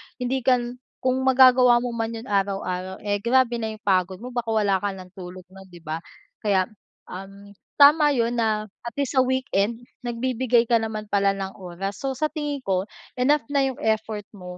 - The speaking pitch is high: Yes, high, 225 Hz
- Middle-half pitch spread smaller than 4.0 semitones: No, average, 4.5 semitones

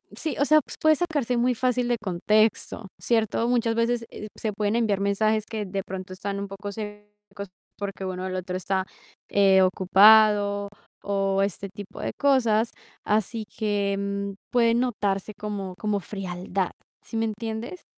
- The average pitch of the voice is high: Yes, high, 210 Hz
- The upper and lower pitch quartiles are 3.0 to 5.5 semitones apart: No, narrow, 2.5 semitones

